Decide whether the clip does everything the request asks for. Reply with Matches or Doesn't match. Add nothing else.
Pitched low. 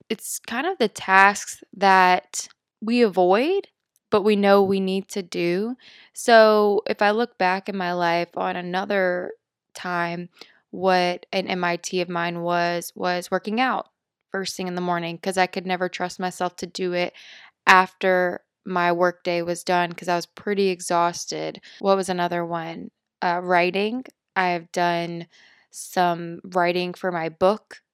Doesn't match